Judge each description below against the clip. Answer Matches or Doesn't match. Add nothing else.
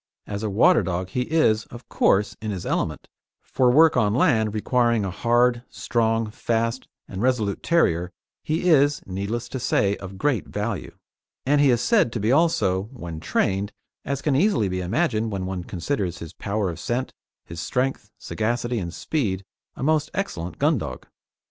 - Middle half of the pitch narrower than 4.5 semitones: Doesn't match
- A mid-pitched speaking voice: Doesn't match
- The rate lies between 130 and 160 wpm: Doesn't match